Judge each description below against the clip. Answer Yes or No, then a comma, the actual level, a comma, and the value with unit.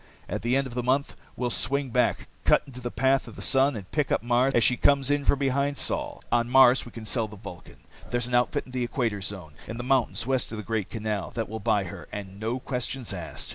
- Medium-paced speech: No, fast, 255 wpm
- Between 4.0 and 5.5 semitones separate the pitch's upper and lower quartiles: No, average, 3.3 semitones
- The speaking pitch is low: Yes, low, 120 Hz